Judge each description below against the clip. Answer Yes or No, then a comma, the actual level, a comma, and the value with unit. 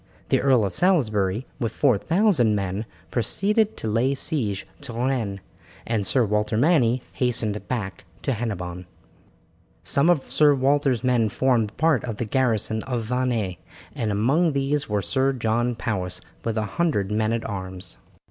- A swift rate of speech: No, average, 155 wpm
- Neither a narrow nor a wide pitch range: Yes, average, 4.4 semitones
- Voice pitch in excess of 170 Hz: No, low, 115 Hz